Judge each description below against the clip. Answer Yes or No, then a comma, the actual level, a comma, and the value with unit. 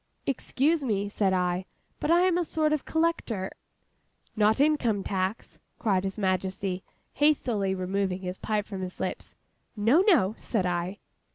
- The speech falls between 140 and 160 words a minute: Yes, average, 150 wpm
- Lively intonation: Yes, wide, 7.2 semitones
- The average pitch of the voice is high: Yes, high, 205 Hz